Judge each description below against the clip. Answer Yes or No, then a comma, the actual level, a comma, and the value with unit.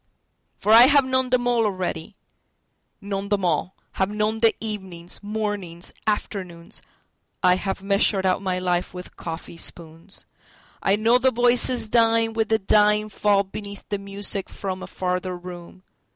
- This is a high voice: Yes, high, 200 Hz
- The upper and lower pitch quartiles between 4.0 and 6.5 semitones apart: No, average, 3.2 semitones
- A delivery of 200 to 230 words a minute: No, slow, 135 wpm